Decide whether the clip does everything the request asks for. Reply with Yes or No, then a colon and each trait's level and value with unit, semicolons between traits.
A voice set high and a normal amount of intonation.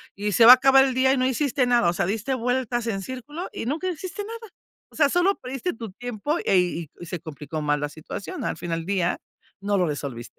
No: high, 235 Hz; wide, 7.4 semitones